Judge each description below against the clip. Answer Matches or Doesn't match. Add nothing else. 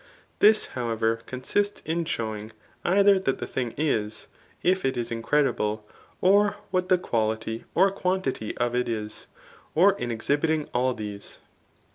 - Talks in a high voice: Doesn't match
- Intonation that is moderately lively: Doesn't match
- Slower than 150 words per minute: Matches